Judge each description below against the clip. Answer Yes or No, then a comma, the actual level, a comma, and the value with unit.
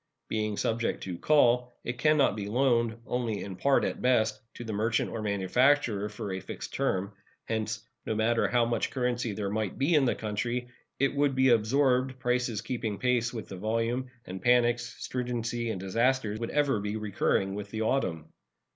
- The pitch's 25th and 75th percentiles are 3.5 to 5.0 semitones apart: No, average, 2.9 semitones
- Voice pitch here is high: No, low, 115 Hz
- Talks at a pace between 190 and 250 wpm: No, average, 180 wpm